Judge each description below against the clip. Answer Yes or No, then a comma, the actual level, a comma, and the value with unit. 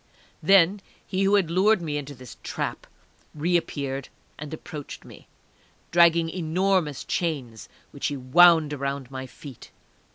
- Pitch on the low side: No, medium, 155 Hz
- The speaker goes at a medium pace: No, slow, 130 wpm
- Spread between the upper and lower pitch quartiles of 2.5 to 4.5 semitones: Yes, average, 4.1 semitones